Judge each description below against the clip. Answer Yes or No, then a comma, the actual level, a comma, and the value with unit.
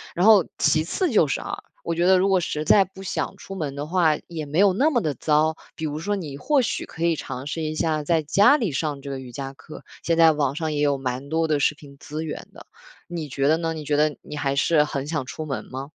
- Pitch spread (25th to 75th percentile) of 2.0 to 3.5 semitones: Yes, average, 3.0 semitones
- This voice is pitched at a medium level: Yes, medium, 155 Hz